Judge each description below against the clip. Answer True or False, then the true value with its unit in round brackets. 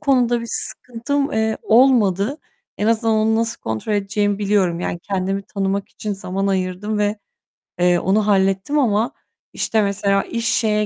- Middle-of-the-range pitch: False (210 Hz)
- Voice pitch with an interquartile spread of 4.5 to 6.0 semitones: False (2.6 semitones)